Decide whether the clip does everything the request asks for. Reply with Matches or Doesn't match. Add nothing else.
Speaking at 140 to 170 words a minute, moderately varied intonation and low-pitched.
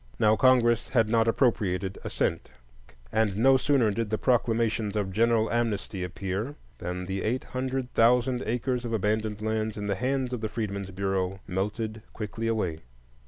Matches